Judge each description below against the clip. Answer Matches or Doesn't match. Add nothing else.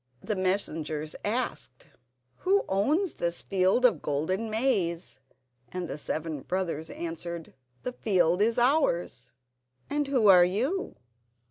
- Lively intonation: Matches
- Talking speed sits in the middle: Doesn't match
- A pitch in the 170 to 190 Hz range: Matches